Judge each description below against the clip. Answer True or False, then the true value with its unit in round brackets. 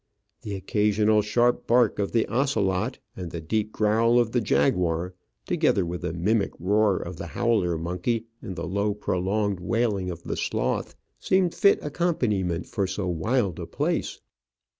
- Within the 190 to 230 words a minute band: False (160 wpm)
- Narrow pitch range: False (4.2 semitones)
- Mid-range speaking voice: False (105 Hz)